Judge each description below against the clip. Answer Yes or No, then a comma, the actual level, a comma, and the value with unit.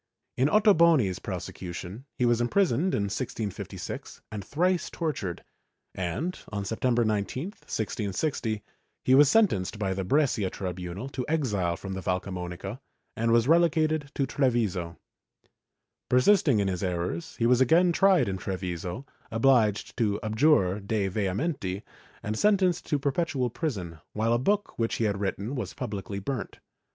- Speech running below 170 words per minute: Yes, average, 145 wpm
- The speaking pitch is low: Yes, low, 115 Hz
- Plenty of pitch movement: Yes, wide, 7.2 semitones